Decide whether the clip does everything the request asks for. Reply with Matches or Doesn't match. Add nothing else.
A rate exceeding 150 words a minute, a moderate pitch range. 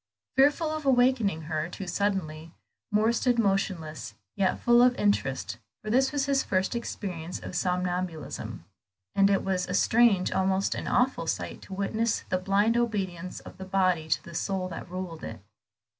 Matches